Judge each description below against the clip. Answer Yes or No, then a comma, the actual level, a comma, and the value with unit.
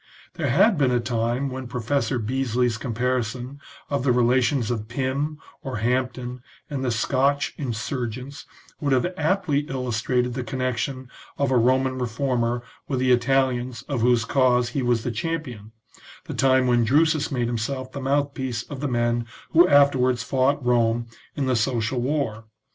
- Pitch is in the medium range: No, low, 125 Hz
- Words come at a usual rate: Yes, average, 155 wpm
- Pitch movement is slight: Yes, narrow, 2.3 semitones